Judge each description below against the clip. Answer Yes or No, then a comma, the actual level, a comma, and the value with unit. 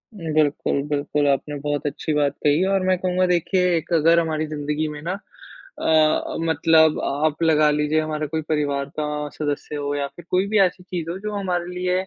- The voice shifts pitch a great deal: No, average, 3.2 semitones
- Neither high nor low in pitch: Yes, medium, 155 Hz